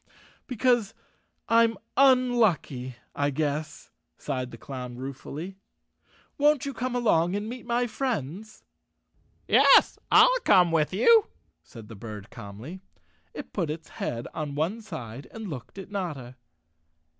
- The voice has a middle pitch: Yes, medium, 175 Hz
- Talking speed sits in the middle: No, slow, 130 wpm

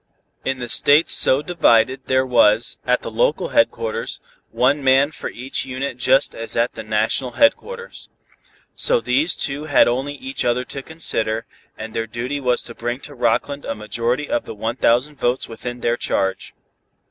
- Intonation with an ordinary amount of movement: Yes, average, 3.5 semitones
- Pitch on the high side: No, low, 130 Hz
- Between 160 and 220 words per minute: Yes, average, 170 wpm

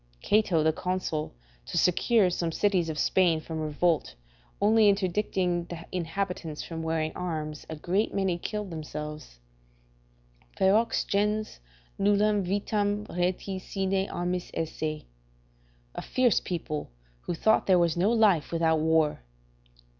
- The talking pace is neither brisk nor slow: No, slow, 125 wpm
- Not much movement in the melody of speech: No, average, 3.8 semitones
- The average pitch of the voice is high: No, medium, 180 Hz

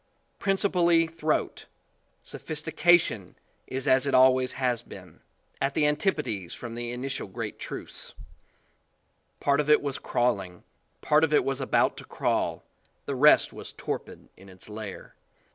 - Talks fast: No, average, 145 wpm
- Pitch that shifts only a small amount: No, average, 4.2 semitones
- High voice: No, low, 135 Hz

